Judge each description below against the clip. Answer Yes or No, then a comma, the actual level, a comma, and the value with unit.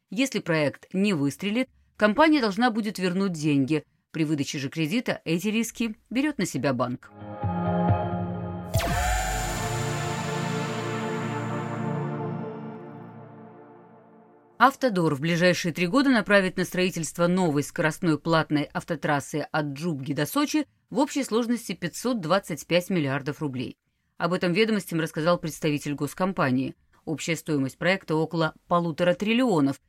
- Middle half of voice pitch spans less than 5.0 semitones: No, average, 5.3 semitones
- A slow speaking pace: Yes, slow, 105 wpm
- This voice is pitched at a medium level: Yes, medium, 170 Hz